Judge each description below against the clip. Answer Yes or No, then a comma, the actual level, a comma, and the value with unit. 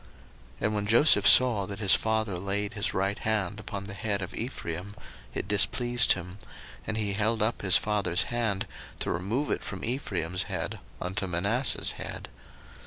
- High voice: No, low, 105 Hz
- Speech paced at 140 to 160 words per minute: No, average, 170 wpm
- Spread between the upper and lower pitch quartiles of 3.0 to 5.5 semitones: No, narrow, 2.4 semitones